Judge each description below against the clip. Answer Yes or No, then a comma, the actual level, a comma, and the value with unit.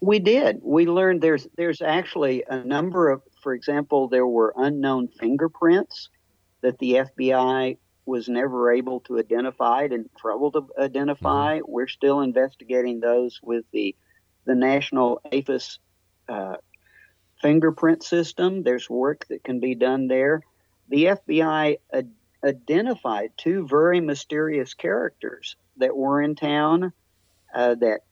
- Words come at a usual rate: No, slow, 130 wpm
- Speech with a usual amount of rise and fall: Yes, average, 3.7 semitones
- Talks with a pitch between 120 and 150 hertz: Yes, low, 135 Hz